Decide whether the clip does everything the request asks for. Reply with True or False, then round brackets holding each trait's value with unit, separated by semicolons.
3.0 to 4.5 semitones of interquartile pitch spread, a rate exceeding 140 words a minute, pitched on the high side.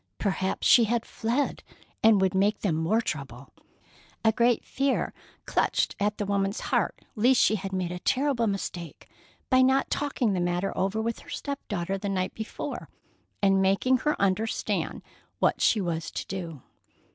True (3.8 semitones; 165 wpm; 200 Hz)